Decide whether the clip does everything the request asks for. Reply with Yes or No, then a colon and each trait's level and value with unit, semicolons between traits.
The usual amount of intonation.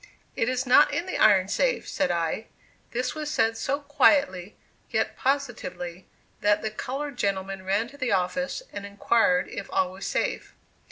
No: wide, 6.3 semitones